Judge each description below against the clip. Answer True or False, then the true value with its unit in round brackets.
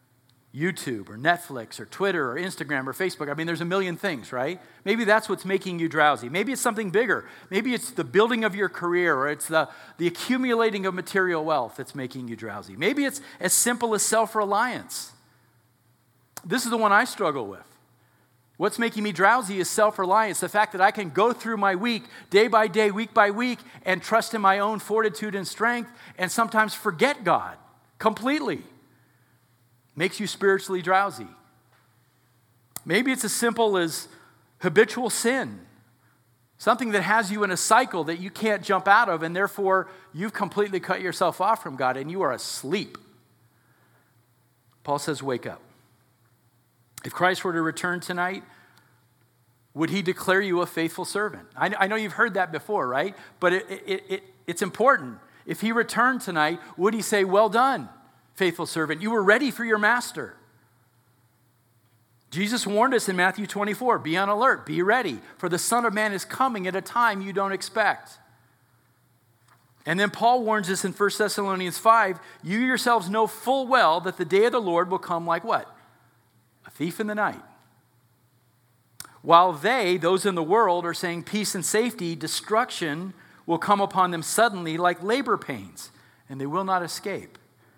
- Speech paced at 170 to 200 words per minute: True (175 wpm)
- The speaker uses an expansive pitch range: True (6.8 semitones)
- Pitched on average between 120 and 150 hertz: False (185 Hz)